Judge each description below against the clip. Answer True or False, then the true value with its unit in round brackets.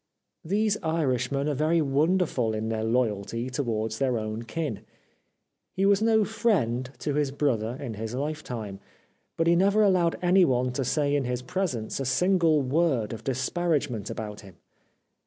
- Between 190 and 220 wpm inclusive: False (155 wpm)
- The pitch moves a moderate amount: False (6.4 semitones)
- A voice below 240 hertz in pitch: True (135 Hz)